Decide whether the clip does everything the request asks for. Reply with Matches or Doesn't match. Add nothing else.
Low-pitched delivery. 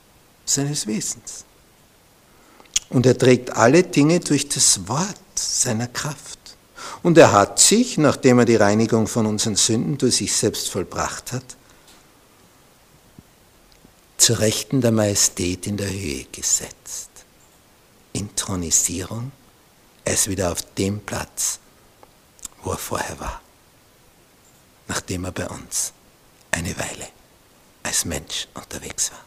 Matches